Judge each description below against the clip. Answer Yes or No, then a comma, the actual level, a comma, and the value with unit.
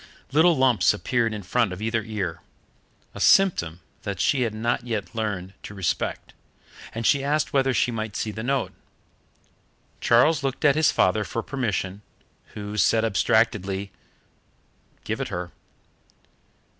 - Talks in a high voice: No, low, 110 Hz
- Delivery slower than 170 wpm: Yes, average, 145 wpm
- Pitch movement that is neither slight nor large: Yes, average, 4.3 semitones